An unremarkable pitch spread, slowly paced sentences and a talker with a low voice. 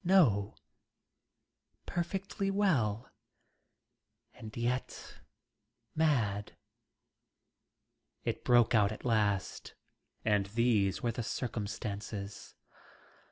Yes: average, 4.0 semitones; slow, 70 wpm; low, 110 Hz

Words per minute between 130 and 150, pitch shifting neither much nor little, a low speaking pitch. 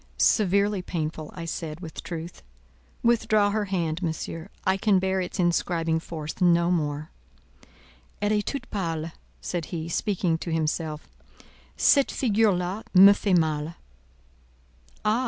No: slow, 135 wpm; average, 3.7 semitones; medium, 175 Hz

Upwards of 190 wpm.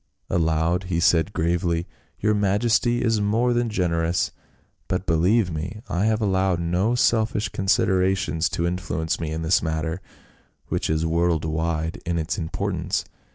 No: average, 145 wpm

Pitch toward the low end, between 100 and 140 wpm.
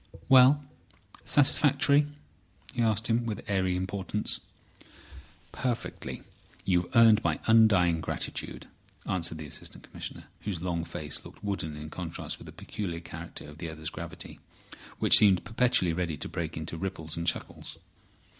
Yes: very low, 90 Hz; slow, 135 wpm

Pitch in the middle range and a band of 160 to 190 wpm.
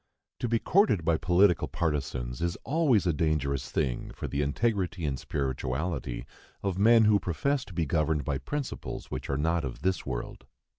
No: very low, 85 Hz; average, 170 wpm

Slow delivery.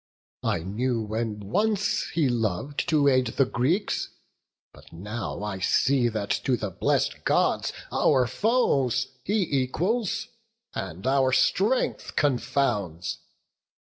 Yes: slow, 115 wpm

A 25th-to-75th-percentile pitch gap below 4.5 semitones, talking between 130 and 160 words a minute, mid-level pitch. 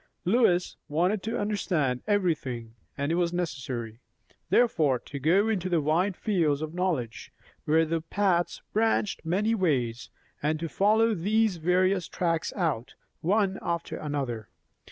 No: average, 5.2 semitones; slow, 135 wpm; medium, 170 Hz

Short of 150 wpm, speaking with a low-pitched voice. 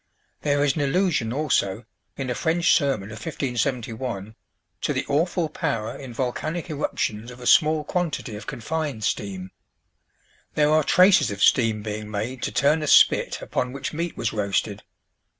No: average, 160 wpm; low, 130 Hz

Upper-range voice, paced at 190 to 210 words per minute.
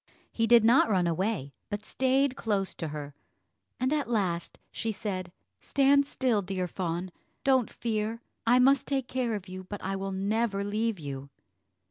No: high, 210 Hz; average, 165 wpm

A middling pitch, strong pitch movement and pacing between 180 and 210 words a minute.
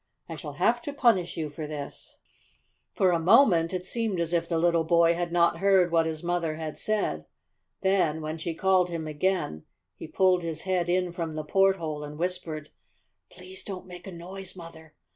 No: medium, 170 Hz; narrow, 2.6 semitones; average, 190 wpm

